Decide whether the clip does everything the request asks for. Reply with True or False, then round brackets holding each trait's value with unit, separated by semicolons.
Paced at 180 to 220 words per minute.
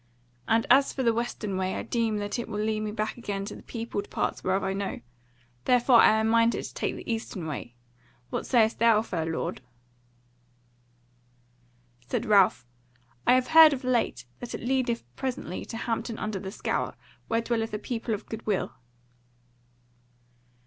False (170 wpm)